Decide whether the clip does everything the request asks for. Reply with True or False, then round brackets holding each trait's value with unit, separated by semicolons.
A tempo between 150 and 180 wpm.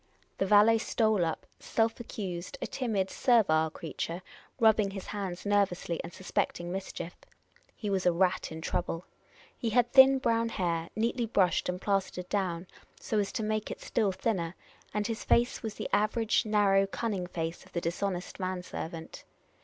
True (165 wpm)